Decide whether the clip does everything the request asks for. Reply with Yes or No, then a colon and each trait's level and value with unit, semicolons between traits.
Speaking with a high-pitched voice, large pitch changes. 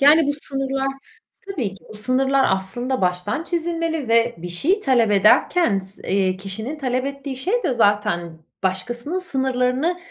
Yes: very high, 255 Hz; wide, 6.4 semitones